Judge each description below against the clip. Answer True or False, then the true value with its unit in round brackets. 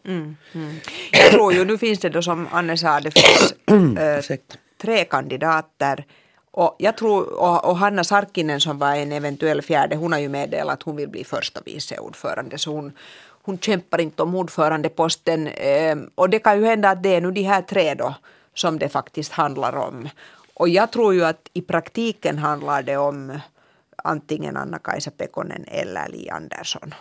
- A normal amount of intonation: True (4.1 semitones)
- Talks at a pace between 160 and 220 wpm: True (180 wpm)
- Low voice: False (165 Hz)